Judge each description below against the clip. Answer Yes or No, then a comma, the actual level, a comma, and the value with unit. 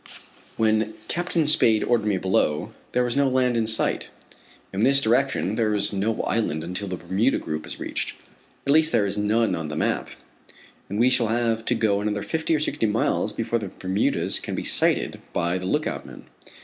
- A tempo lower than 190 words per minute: No, average, 195 wpm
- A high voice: No, low, 110 Hz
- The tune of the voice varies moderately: Yes, average, 3.7 semitones